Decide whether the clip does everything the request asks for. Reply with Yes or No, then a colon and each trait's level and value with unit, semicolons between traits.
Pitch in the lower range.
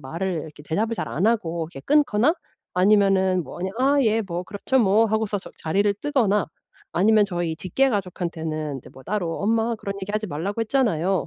No: high, 195 Hz